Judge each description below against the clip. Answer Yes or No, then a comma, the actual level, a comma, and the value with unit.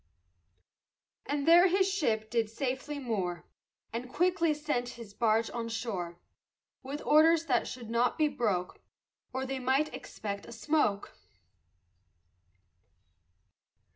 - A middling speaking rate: No, slow, 115 wpm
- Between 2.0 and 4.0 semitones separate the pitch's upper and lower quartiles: No, average, 5.1 semitones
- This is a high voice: Yes, very high, 250 Hz